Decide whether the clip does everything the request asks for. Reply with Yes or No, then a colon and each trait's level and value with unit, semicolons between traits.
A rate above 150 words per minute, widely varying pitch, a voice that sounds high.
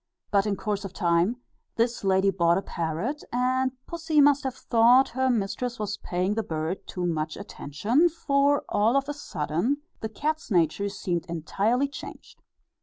Yes: average, 165 wpm; wide, 6.6 semitones; high, 215 Hz